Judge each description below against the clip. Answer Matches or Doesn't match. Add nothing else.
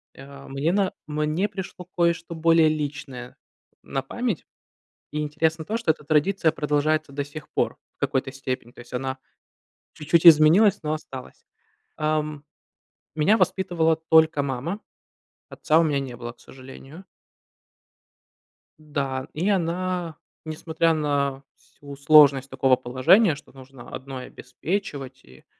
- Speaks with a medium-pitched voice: Matches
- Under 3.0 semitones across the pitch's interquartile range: Doesn't match